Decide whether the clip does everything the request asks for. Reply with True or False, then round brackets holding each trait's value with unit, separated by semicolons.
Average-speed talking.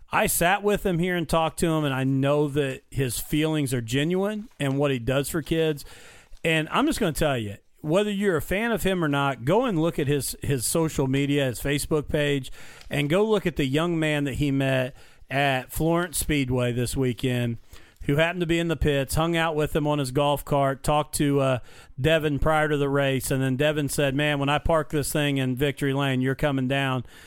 False (225 wpm)